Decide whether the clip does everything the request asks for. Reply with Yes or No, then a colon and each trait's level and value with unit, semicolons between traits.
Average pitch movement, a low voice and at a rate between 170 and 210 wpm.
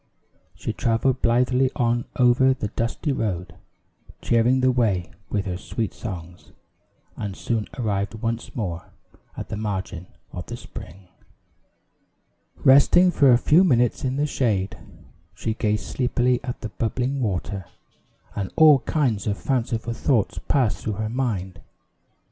No: average, 4.2 semitones; low, 115 Hz; slow, 135 wpm